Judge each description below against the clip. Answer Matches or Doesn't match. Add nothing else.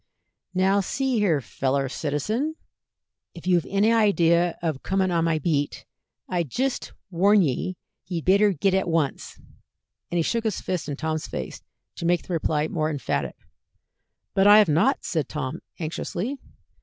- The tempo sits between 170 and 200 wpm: Doesn't match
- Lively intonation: Doesn't match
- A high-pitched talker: Doesn't match